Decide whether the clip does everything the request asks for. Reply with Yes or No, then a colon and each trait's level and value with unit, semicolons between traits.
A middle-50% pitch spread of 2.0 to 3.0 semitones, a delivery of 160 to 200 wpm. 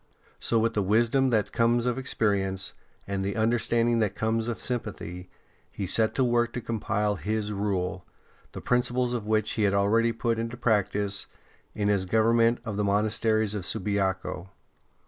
Yes: narrow, 2.5 semitones; average, 165 wpm